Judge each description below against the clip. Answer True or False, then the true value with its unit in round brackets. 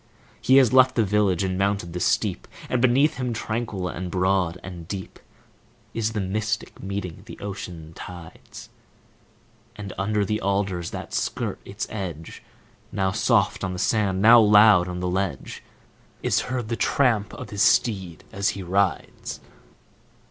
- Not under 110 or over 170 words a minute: True (155 wpm)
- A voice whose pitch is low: True (100 Hz)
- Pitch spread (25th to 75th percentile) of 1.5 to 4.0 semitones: True (2.9 semitones)